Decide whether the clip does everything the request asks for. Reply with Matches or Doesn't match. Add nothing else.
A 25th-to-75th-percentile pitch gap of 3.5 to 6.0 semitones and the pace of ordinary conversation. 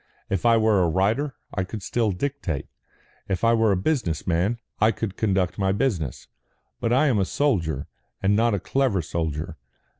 Matches